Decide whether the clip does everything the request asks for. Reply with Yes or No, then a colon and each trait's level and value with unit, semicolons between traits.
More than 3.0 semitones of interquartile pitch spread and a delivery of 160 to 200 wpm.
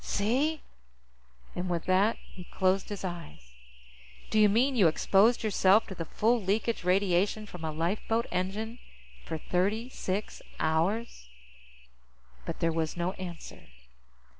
No: average, 3.8 semitones; slow, 135 wpm